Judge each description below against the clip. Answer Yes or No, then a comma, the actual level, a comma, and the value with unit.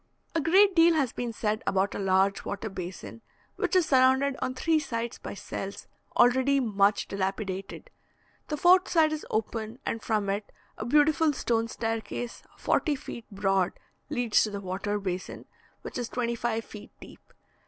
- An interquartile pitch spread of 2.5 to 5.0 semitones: No, wide, 5.6 semitones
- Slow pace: No, average, 165 wpm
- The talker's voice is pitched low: No, high, 230 Hz